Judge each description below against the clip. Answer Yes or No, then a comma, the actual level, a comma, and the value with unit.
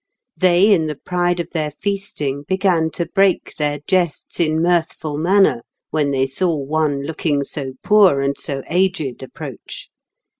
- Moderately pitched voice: Yes, medium, 160 Hz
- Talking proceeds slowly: No, average, 150 wpm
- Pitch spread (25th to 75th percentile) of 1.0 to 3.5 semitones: No, average, 4.2 semitones